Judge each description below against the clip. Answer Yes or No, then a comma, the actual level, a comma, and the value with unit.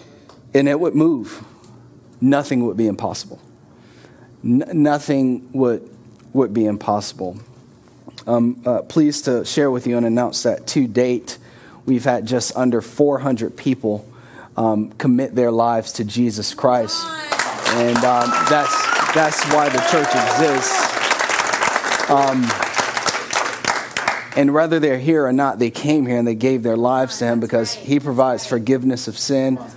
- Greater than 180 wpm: No, average, 145 wpm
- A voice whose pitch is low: Yes, low, 125 Hz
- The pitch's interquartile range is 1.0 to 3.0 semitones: Yes, narrow, 2.6 semitones